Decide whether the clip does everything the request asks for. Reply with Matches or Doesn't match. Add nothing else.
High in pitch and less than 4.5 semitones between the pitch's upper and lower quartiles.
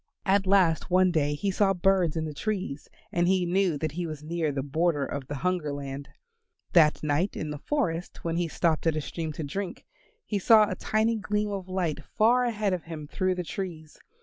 Doesn't match